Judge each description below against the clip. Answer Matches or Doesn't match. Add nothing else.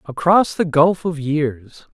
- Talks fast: Doesn't match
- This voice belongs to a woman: Doesn't match